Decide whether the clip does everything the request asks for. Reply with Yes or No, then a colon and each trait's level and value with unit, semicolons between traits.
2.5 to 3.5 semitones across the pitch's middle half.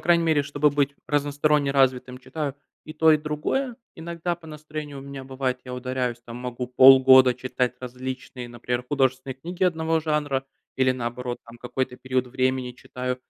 Yes: average, 3.1 semitones